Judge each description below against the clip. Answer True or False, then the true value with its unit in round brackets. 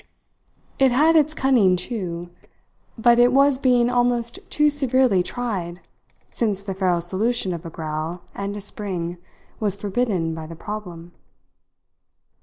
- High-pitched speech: True (205 Hz)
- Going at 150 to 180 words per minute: False (135 wpm)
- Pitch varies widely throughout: True (5.8 semitones)